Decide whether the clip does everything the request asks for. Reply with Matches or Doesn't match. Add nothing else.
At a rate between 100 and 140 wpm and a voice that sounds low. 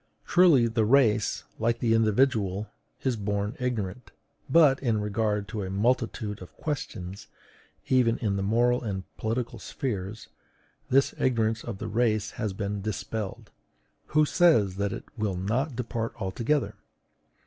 Matches